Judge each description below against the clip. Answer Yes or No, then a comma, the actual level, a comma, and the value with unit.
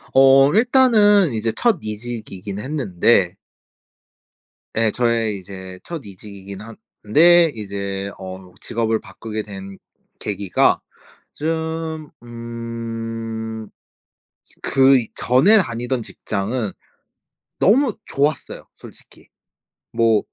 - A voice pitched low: Yes, low, 115 Hz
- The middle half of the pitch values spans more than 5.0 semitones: Yes, wide, 5.5 semitones